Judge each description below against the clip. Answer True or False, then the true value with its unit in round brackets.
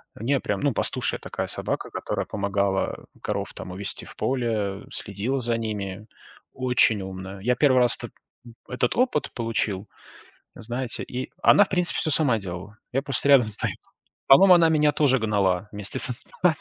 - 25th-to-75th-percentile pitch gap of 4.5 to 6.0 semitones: True (5.1 semitones)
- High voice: False (115 Hz)